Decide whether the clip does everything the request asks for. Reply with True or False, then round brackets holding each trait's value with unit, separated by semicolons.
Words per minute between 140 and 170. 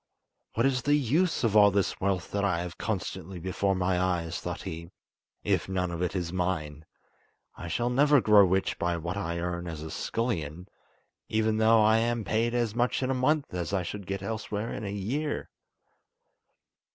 False (190 wpm)